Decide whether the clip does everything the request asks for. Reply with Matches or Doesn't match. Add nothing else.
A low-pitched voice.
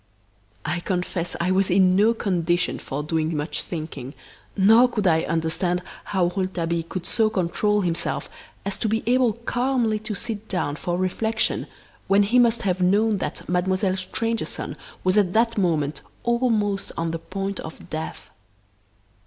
Doesn't match